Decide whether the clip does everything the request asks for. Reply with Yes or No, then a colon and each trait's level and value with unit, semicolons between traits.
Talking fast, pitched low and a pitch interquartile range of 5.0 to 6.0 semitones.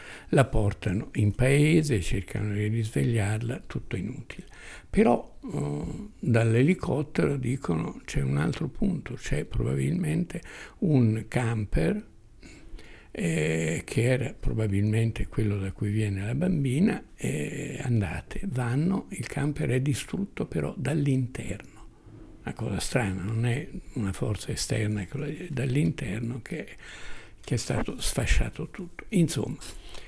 No: slow, 115 wpm; low, 120 Hz; wide, 5.6 semitones